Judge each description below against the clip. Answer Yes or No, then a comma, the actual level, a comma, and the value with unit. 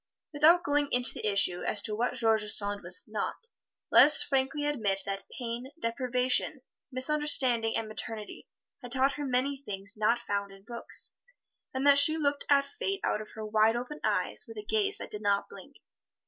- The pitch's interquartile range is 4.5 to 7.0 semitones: Yes, average, 4.9 semitones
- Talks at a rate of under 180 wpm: No, average, 185 wpm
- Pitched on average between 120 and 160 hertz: No, very high, 250 Hz